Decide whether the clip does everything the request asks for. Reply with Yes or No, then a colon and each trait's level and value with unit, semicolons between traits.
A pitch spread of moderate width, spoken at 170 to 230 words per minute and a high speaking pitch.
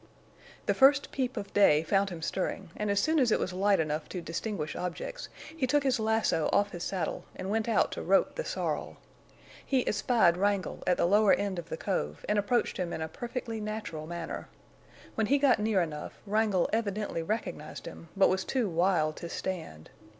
Yes: average, 4.6 semitones; average, 195 wpm; high, 200 Hz